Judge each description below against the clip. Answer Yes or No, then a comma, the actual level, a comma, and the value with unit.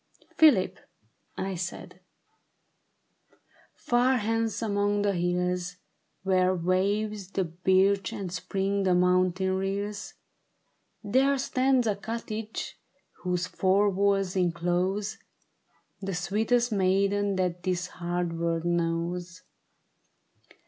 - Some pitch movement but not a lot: No, narrow, 2.3 semitones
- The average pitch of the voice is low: No, high, 190 Hz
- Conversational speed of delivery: No, slow, 100 wpm